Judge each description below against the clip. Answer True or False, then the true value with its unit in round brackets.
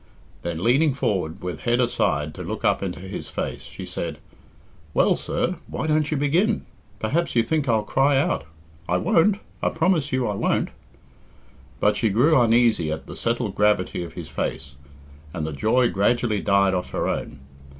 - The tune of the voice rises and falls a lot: True (7.4 semitones)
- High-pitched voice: False (115 Hz)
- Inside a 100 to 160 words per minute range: False (175 wpm)